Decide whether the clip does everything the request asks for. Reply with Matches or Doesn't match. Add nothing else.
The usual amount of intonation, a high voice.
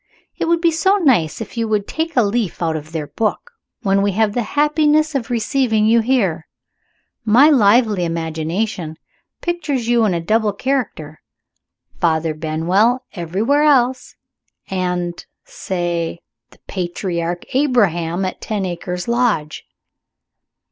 Doesn't match